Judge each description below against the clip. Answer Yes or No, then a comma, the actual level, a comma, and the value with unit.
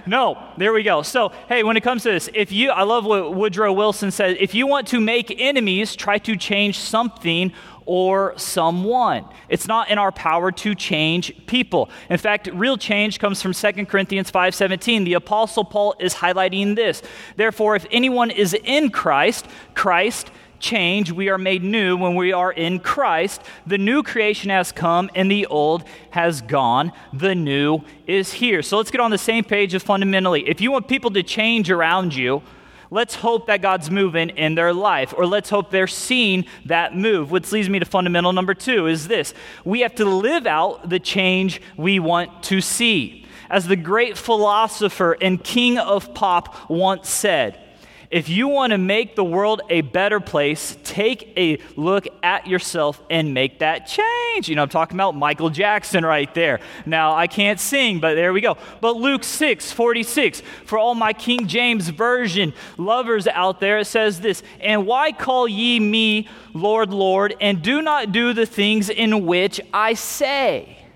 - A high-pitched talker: Yes, high, 200 Hz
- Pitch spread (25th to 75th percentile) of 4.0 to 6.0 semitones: No, average, 3.6 semitones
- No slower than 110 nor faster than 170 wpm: No, average, 185 wpm